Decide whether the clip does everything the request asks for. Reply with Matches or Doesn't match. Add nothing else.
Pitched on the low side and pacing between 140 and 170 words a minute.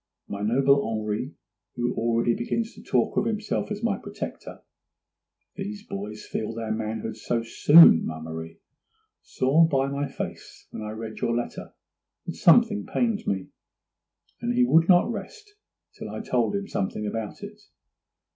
Matches